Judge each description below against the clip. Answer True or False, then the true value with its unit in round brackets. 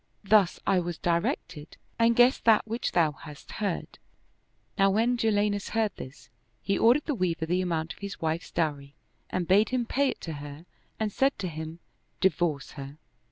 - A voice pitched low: False (185 Hz)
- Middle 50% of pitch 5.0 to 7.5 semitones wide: True (5.3 semitones)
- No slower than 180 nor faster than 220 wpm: True (190 wpm)